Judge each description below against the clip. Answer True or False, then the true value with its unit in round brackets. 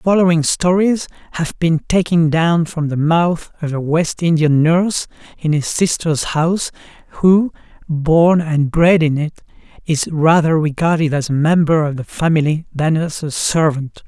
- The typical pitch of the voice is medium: True (160 Hz)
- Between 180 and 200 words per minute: False (160 wpm)